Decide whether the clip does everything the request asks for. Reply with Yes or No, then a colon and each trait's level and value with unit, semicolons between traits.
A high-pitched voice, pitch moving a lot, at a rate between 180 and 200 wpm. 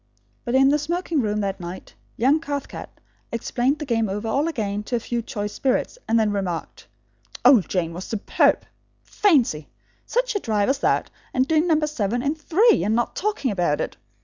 Yes: high, 240 Hz; wide, 6.5 semitones; average, 185 wpm